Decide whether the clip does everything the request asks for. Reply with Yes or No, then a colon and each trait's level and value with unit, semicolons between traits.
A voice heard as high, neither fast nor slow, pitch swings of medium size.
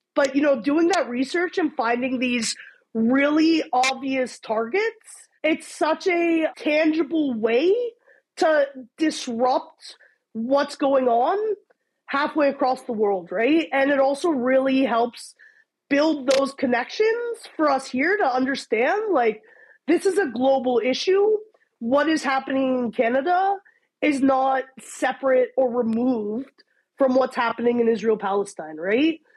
No: very high, 275 Hz; slow, 130 wpm; average, 4.5 semitones